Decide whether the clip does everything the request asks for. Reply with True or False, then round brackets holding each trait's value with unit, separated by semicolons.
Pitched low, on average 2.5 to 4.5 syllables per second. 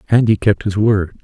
False (105 Hz; 5.0 syllables/s)